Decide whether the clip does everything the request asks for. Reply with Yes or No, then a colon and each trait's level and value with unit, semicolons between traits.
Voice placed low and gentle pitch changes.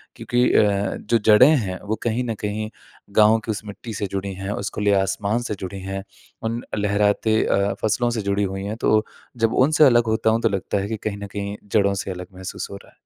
Yes: low, 105 Hz; narrow, 2.1 semitones